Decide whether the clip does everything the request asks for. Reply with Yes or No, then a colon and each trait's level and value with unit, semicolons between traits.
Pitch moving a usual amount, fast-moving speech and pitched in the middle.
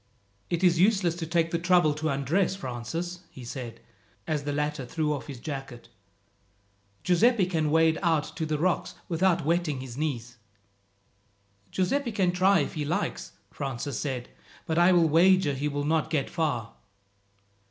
No: average, 3.9 semitones; average, 160 wpm; medium, 160 Hz